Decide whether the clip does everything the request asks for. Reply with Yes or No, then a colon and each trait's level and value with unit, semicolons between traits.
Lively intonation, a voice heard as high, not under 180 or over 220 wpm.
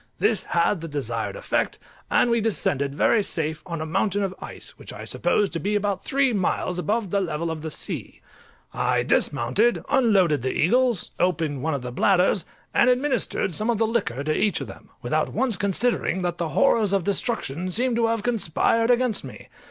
Yes: wide, 6.2 semitones; high, 195 Hz; average, 190 wpm